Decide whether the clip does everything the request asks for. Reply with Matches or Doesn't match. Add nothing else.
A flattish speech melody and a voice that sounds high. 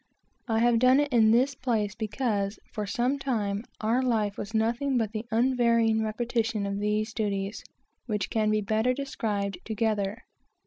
Matches